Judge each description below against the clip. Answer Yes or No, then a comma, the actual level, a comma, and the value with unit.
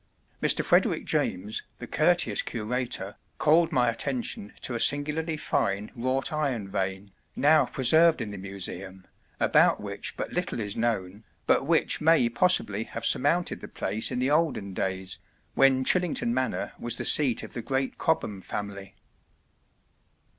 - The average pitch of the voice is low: Yes, low, 120 Hz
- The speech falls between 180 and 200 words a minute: No, average, 145 wpm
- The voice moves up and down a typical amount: No, wide, 6.1 semitones